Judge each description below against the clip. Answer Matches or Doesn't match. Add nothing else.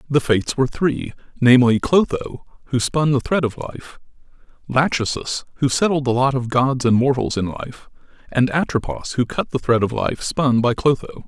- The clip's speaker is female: Doesn't match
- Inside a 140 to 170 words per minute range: Doesn't match